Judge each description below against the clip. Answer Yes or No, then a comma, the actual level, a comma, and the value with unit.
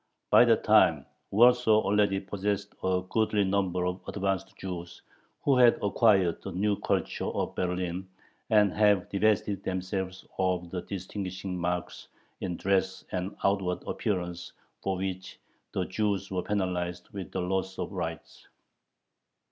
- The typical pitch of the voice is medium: No, very low, 95 Hz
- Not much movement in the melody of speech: Yes, narrow, 1.9 semitones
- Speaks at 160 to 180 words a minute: No, slow, 135 wpm